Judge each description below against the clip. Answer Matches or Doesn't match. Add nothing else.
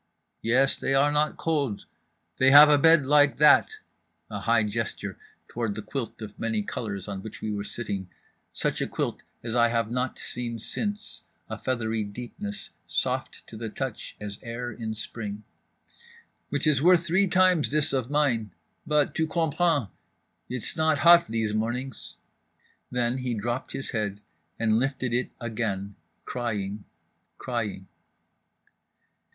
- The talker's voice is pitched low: Matches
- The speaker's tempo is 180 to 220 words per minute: Doesn't match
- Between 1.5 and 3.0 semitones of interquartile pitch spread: Doesn't match